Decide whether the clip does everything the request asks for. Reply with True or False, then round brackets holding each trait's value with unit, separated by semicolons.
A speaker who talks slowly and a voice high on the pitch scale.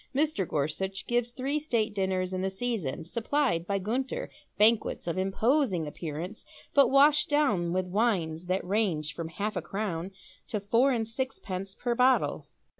False (155 wpm; 205 Hz)